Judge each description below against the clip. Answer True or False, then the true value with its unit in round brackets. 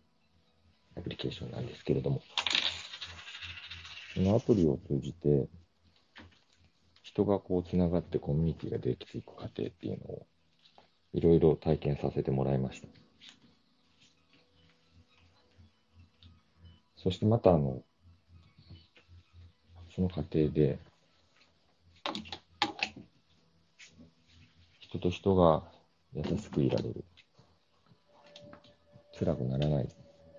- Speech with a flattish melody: True (2.3 semitones)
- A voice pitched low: True (85 Hz)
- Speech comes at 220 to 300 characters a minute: False (195 characters per minute)